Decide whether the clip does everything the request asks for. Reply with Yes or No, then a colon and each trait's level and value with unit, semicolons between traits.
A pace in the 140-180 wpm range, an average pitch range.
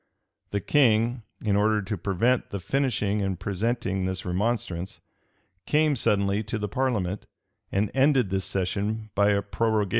Yes: average, 150 wpm; average, 3.2 semitones